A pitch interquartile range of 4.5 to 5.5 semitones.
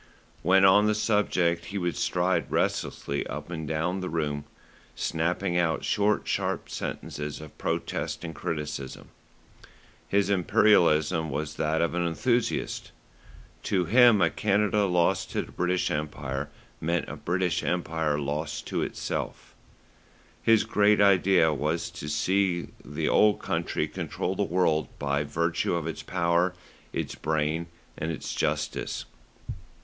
No: average, 3.7 semitones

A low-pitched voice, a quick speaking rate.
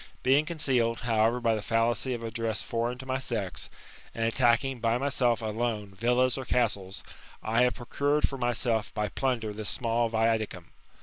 No: low, 115 Hz; average, 170 wpm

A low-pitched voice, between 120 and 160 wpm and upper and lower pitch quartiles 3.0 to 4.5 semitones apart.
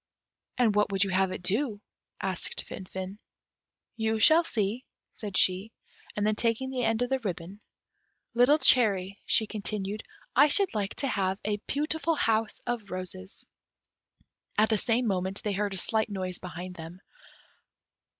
No: high, 210 Hz; average, 155 wpm; average, 3.7 semitones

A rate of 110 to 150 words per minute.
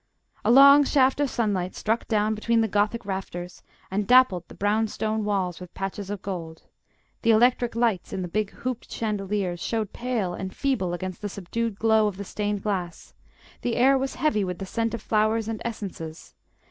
No: average, 185 wpm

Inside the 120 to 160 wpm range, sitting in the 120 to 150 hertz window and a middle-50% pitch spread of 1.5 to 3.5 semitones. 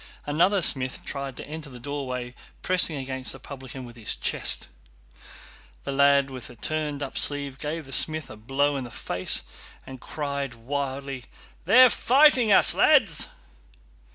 Yes: average, 155 wpm; medium, 140 Hz; narrow, 2.4 semitones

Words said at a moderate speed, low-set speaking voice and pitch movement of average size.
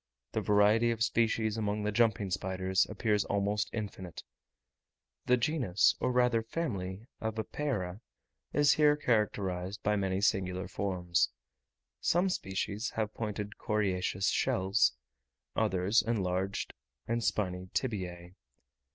No: slow, 115 wpm; low, 105 Hz; average, 3.2 semitones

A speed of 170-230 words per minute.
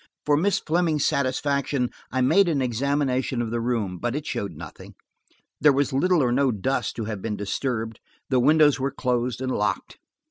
Yes: average, 180 wpm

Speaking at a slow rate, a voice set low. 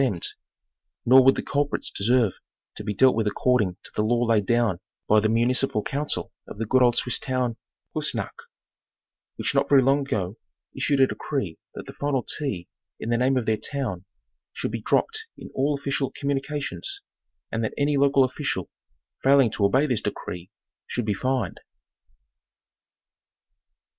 No: average, 170 wpm; low, 125 Hz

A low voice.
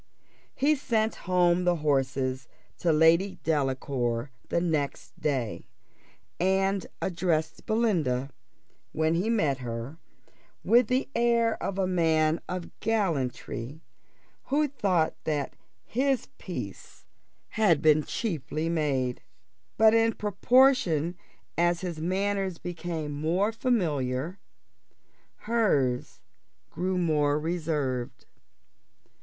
No: medium, 170 Hz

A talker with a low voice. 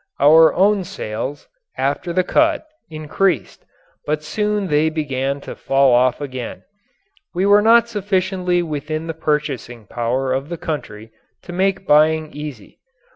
No: medium, 155 Hz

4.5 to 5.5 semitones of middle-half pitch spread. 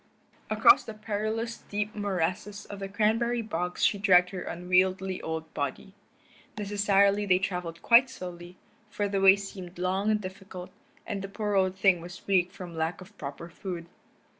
No: narrow, 2.5 semitones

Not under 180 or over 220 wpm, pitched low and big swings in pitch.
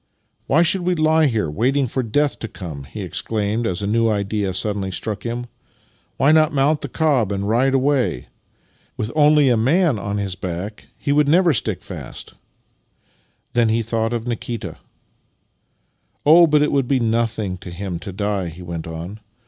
Yes: average, 195 wpm; low, 115 Hz; wide, 6.0 semitones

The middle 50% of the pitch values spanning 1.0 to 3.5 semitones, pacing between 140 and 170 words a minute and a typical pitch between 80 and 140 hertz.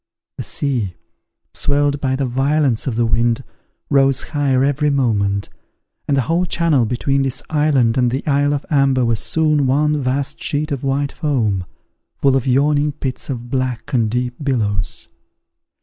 Yes: average, 2.9 semitones; average, 160 wpm; low, 135 Hz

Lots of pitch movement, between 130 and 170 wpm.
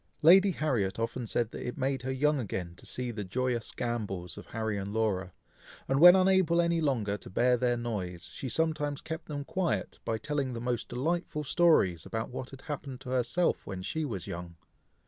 No: wide, 5.7 semitones; average, 195 wpm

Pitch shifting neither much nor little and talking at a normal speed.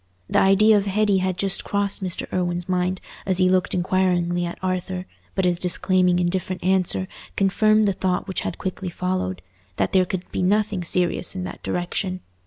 No: narrow, 1.3 semitones; average, 175 wpm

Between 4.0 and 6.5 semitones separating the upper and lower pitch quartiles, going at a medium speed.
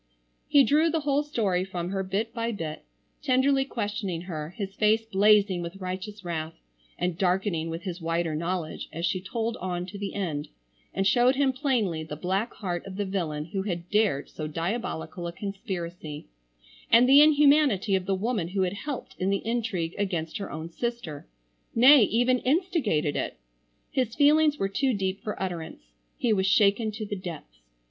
Yes: average, 5.3 semitones; average, 175 wpm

